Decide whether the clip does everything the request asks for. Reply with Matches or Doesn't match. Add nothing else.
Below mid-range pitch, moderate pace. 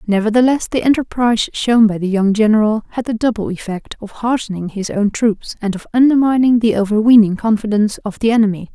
Doesn't match